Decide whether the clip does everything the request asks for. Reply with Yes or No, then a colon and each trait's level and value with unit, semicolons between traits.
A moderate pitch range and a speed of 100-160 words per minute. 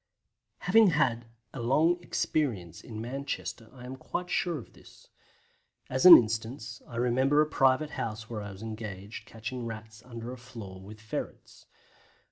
Yes: average, 3.7 semitones; average, 155 wpm